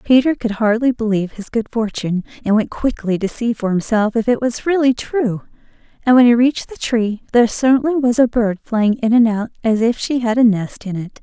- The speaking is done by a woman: Yes, female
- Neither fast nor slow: No, fast, 225 wpm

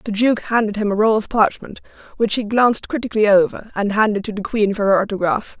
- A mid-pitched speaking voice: No, high, 210 Hz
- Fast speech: Yes, fast, 225 wpm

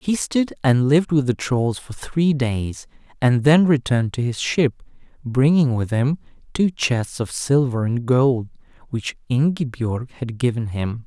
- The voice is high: No, low, 130 Hz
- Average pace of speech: Yes, average, 165 wpm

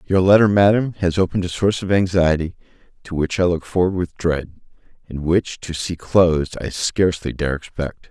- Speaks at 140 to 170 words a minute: No, average, 185 wpm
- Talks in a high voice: No, very low, 90 Hz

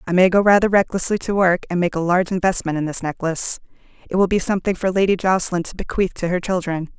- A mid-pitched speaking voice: Yes, medium, 180 Hz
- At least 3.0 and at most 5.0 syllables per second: No, 6.8 syllables/s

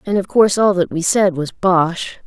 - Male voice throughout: No, female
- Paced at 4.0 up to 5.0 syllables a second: Yes, 4.8 syllables/s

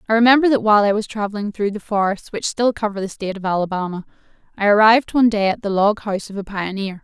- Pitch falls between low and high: No, high, 210 Hz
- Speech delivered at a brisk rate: Yes, fast, 240 wpm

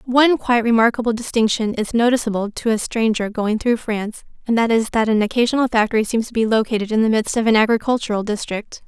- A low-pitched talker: No, high, 225 Hz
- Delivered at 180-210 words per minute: Yes, fast, 205 wpm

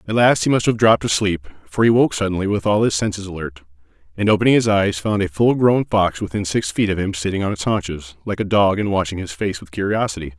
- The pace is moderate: No, fast, 250 wpm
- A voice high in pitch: No, very low, 95 Hz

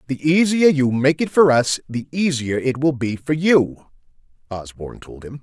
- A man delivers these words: Yes, male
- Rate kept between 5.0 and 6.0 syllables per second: No, 4.6 syllables/s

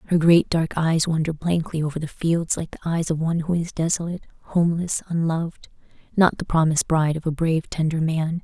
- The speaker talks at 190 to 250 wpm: Yes, average, 200 wpm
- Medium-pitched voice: Yes, medium, 165 Hz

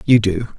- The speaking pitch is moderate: No, low, 110 Hz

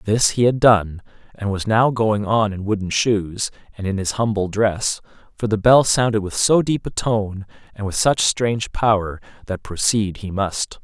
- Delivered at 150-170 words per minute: No, average, 195 wpm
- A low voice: Yes, low, 105 Hz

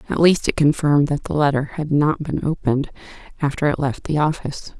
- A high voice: No, medium, 145 Hz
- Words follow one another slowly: No, average, 200 wpm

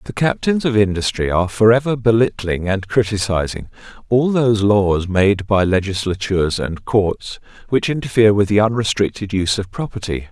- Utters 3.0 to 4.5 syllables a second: No, 5.3 syllables/s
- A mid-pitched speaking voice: No, low, 105 Hz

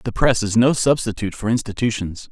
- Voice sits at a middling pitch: No, low, 110 Hz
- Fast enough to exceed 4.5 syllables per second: Yes, 5.9 syllables/s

